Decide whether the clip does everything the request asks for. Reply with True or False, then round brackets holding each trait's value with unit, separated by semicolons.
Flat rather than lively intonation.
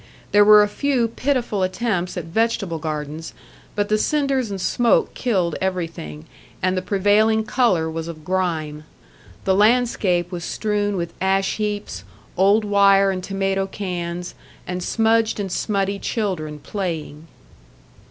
False (3.5 semitones)